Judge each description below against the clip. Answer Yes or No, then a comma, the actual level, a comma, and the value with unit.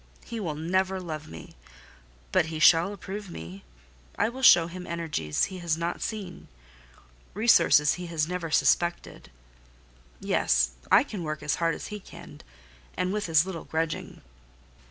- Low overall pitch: No, medium, 170 Hz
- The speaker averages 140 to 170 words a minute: Yes, average, 155 wpm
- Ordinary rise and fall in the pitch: Yes, average, 3.3 semitones